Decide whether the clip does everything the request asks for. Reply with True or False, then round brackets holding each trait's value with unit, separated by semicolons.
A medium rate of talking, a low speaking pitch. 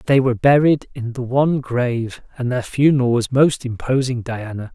True (175 wpm; 125 Hz)